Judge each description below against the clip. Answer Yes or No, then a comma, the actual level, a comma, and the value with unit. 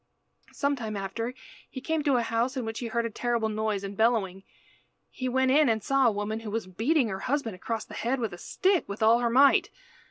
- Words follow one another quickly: Yes, fast, 230 wpm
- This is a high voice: Yes, high, 230 Hz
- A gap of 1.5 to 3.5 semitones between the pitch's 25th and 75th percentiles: Yes, average, 3.2 semitones